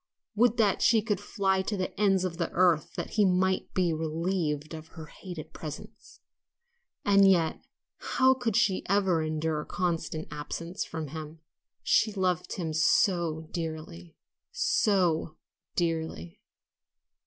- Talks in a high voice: No, medium, 175 Hz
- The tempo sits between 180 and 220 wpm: No, slow, 135 wpm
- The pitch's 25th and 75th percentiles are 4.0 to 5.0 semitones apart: No, average, 3.4 semitones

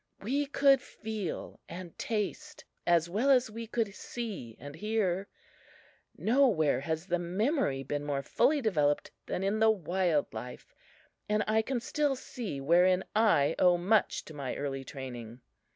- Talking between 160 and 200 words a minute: No, average, 150 wpm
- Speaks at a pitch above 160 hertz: Yes, high, 190 Hz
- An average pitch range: No, wide, 7.2 semitones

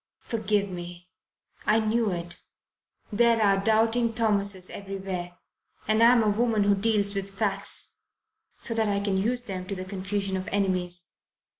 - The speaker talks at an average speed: Yes, average, 150 wpm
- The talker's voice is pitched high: Yes, high, 200 Hz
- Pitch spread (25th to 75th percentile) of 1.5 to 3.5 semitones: Yes, narrow, 2.6 semitones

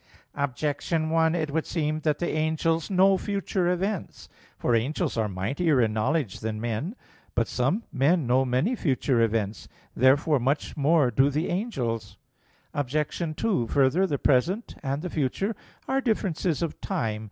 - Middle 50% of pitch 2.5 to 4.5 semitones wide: No, wide, 5.4 semitones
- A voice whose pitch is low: No, medium, 150 Hz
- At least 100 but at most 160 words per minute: Yes, average, 150 wpm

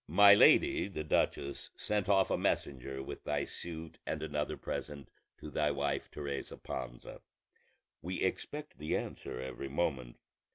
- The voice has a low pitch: Yes, very low, 75 Hz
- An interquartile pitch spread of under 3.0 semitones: No, average, 4.0 semitones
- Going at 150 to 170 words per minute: No, average, 140 wpm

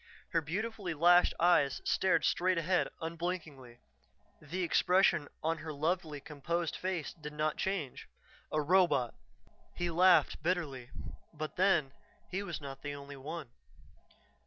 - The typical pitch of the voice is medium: Yes, medium, 165 Hz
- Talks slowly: Yes, slow, 130 wpm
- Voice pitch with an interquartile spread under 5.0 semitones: Yes, average, 3.5 semitones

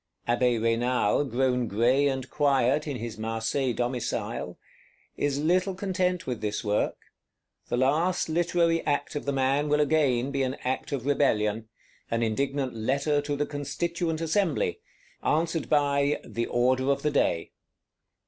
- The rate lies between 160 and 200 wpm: No, average, 145 wpm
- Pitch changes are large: No, average, 3.6 semitones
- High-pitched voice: No, medium, 140 Hz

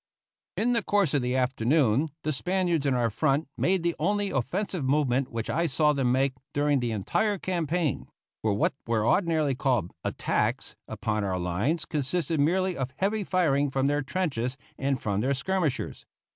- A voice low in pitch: No, medium, 145 Hz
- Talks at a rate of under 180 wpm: Yes, average, 170 wpm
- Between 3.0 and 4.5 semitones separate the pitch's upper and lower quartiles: No, average, 5.3 semitones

